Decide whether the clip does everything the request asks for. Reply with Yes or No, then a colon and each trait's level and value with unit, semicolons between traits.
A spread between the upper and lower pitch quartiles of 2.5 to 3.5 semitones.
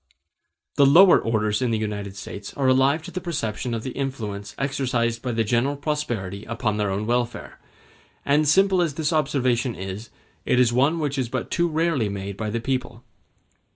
No: average, 4.7 semitones